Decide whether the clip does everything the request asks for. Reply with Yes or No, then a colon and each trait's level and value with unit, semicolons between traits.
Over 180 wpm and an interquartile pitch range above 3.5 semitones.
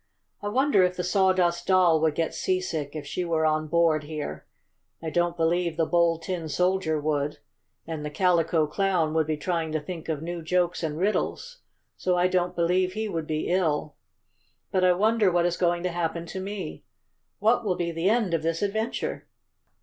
No: average, 190 wpm; narrow, 2.6 semitones